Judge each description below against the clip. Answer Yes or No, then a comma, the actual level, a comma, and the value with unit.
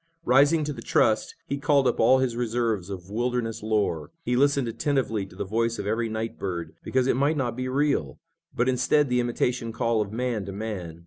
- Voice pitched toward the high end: No, low, 115 Hz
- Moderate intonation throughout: Yes, average, 3.3 semitones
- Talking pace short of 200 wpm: No, fast, 205 wpm